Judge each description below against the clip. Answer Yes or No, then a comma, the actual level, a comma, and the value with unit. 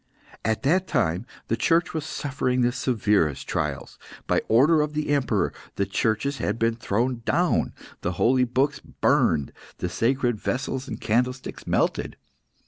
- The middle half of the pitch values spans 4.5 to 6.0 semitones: No, average, 4.1 semitones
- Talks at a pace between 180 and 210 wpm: No, average, 145 wpm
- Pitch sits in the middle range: No, low, 125 Hz